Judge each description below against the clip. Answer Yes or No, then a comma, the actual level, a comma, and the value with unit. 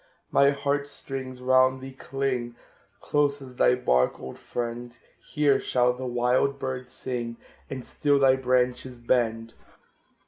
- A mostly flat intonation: Yes, narrow, 1.8 semitones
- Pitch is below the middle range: Yes, low, 130 Hz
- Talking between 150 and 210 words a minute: No, slow, 135 wpm